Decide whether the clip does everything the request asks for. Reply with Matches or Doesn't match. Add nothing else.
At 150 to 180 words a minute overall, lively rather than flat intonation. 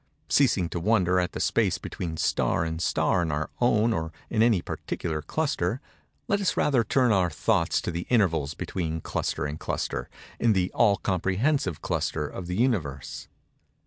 Matches